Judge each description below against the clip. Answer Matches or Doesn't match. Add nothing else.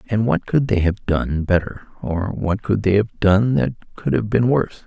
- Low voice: Matches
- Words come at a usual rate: Doesn't match